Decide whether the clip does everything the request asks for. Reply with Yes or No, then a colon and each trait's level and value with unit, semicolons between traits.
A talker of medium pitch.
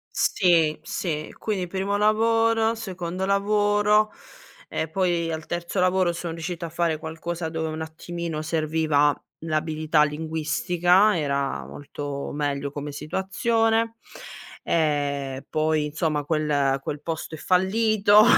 Yes: medium, 165 Hz